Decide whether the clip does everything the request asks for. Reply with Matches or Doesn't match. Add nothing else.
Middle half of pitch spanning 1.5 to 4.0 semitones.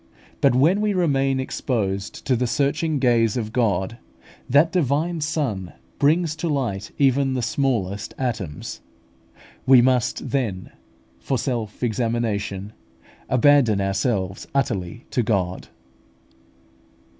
Doesn't match